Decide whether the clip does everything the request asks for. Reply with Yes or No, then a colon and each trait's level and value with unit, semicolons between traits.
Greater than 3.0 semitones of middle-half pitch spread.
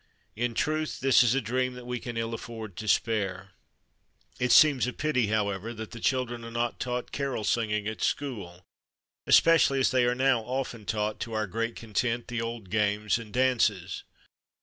No: average, 2.7 semitones